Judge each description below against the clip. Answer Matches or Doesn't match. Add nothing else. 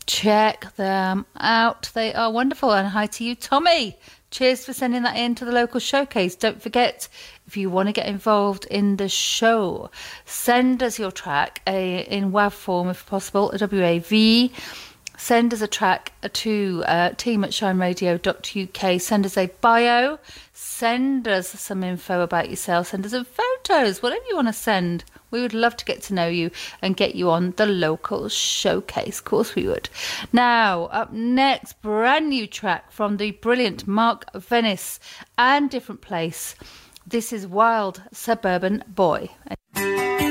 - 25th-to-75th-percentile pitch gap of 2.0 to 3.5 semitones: Doesn't match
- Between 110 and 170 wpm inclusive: Matches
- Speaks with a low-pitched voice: Doesn't match